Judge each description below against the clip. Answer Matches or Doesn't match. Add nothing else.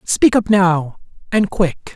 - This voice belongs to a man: Matches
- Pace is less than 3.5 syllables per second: Matches